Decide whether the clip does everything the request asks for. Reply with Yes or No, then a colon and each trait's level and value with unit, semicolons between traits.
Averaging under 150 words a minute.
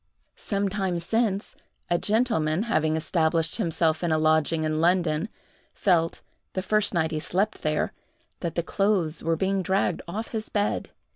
No: average, 155 wpm